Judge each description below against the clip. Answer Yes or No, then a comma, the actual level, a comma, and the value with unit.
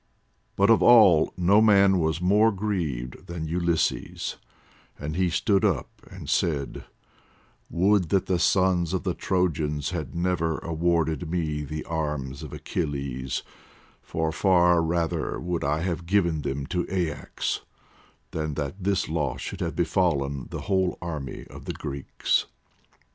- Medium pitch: No, very low, 85 Hz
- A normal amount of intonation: Yes, average, 3.4 semitones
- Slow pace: No, average, 145 wpm